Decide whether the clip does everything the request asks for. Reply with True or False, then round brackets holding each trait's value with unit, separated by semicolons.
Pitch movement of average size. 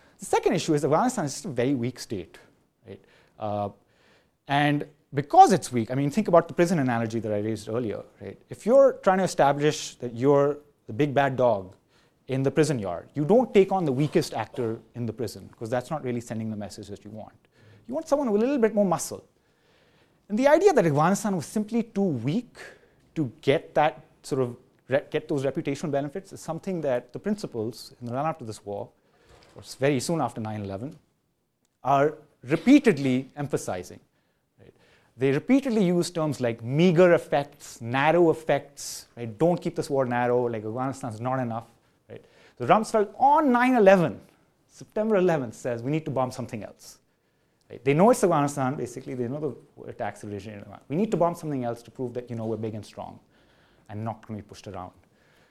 False (6.1 semitones)